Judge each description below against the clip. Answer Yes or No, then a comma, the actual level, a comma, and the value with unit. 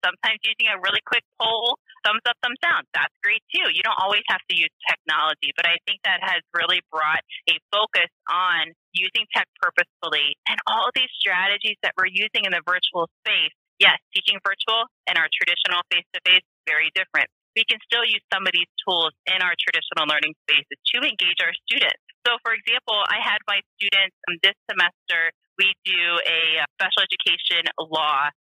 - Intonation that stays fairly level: No, average, 4.5 semitones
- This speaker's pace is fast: No, average, 180 wpm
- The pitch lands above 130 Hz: Yes, high, 190 Hz